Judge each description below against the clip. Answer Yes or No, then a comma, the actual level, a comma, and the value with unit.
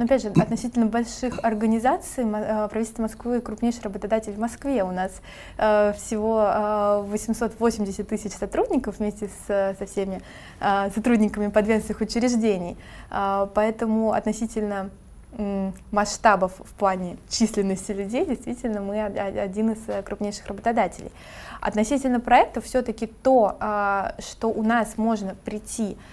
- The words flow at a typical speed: No, slow, 105 wpm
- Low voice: No, high, 215 Hz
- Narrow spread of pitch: Yes, narrow, 2.0 semitones